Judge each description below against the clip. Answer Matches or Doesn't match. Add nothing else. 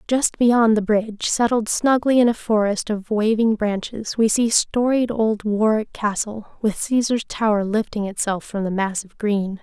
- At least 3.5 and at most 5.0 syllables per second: Matches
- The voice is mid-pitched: Doesn't match